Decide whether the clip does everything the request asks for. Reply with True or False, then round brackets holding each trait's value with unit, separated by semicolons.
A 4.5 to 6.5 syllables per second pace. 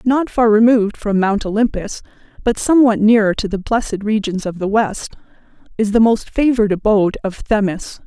True (5.4 syllables/s)